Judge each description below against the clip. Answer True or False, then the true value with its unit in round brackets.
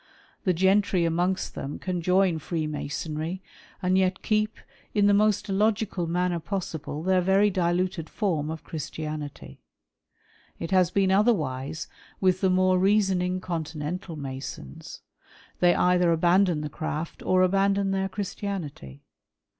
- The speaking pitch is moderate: True (180 Hz)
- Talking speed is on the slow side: True (125 wpm)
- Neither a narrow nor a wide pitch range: True (3.2 semitones)